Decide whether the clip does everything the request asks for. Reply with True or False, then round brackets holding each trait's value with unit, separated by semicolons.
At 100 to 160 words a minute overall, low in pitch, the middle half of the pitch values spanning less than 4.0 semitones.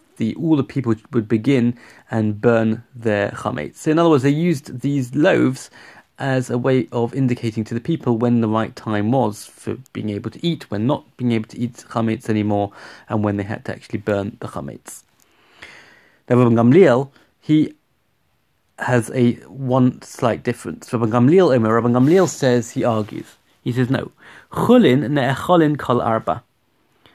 True (155 wpm; 120 Hz; 3.0 semitones)